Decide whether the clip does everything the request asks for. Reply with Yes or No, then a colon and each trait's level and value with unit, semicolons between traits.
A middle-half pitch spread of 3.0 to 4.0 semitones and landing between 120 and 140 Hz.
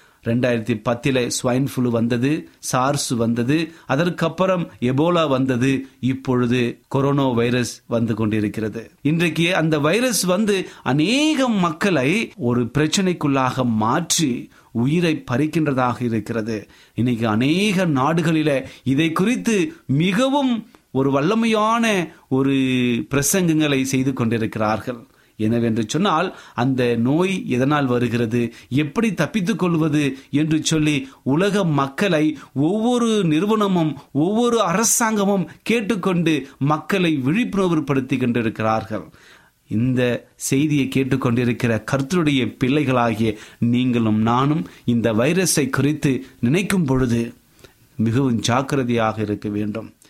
No: average, 5.3 semitones; low, 135 Hz